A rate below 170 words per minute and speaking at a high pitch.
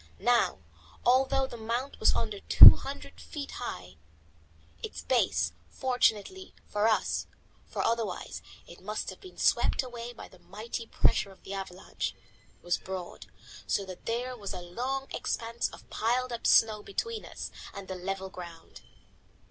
Yes: average, 150 wpm; high, 220 Hz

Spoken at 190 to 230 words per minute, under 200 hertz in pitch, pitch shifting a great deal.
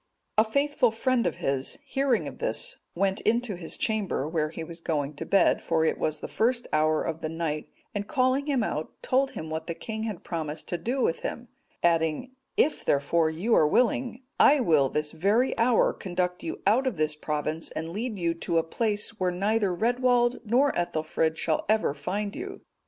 Yes: average, 195 wpm; high, 190 Hz; wide, 7.0 semitones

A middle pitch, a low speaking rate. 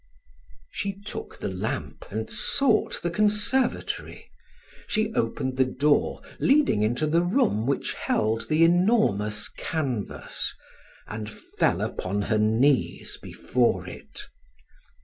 Yes: medium, 150 Hz; slow, 110 wpm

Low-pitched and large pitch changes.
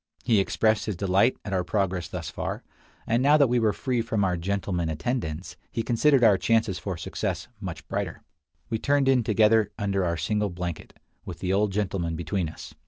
No: low, 100 Hz; average, 4.1 semitones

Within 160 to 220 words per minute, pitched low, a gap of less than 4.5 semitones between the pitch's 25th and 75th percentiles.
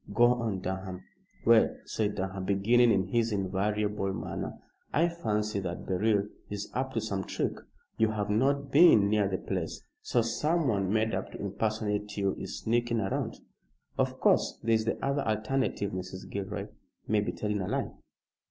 Yes: average, 165 wpm; low, 105 Hz; average, 2.9 semitones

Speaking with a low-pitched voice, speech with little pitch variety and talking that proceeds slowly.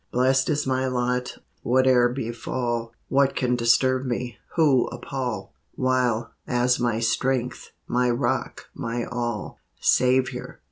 Yes: low, 125 Hz; narrow, 1.6 semitones; slow, 120 wpm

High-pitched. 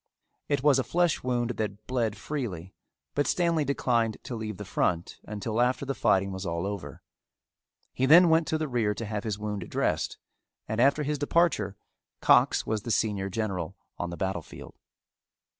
No: low, 110 Hz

